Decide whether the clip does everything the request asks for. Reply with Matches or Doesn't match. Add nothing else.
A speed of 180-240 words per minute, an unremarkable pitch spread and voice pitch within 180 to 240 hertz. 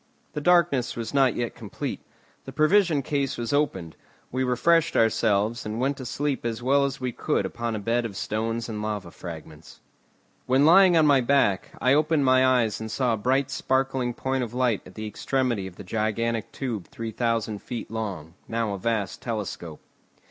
Doesn't match